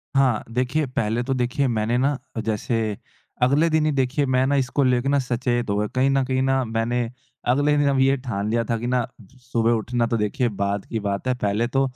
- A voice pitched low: Yes, low, 125 Hz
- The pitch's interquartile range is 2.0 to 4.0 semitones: Yes, average, 2.9 semitones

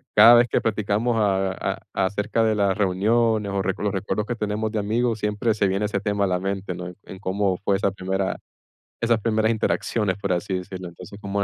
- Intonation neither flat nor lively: No, narrow, 2.3 semitones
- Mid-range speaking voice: No, low, 100 Hz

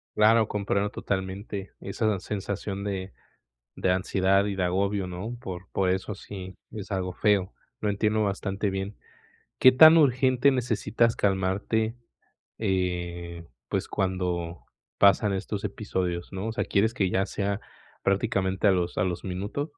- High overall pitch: No, low, 100 Hz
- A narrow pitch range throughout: Yes, narrow, 2.2 semitones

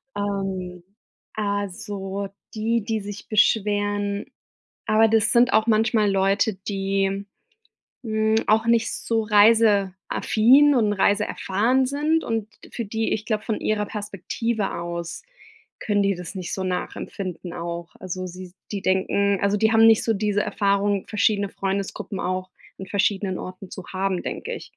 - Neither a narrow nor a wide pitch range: No, narrow, 2.2 semitones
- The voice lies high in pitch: Yes, high, 205 Hz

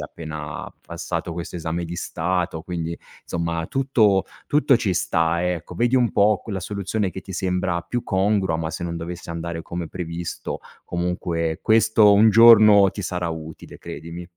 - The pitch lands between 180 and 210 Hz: No, very low, 90 Hz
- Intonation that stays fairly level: No, average, 3.5 semitones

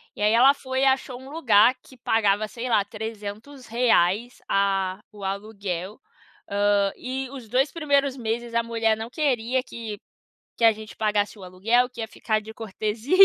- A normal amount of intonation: Yes, average, 3.4 semitones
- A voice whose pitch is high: Yes, high, 225 Hz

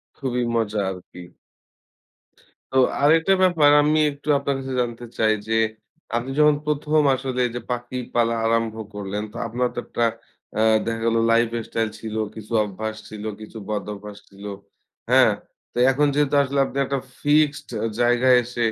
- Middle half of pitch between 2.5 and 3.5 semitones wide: No, average, 4.2 semitones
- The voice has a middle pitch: No, low, 120 Hz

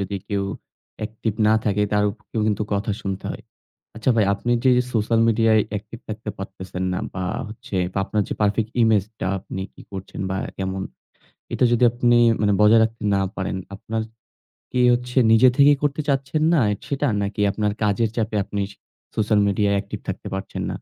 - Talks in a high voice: No, low, 110 Hz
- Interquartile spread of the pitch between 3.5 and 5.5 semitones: No, narrow, 2.5 semitones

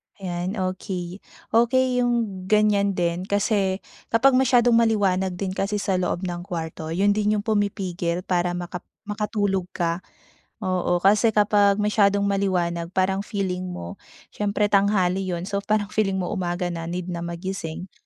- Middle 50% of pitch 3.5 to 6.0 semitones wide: No, average, 2.7 semitones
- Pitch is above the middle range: Yes, high, 195 Hz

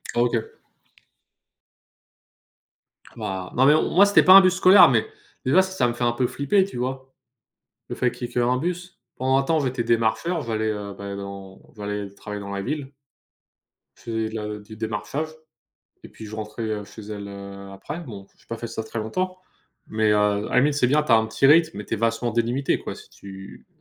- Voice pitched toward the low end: Yes, low, 115 Hz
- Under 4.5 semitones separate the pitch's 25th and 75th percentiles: No, average, 4.9 semitones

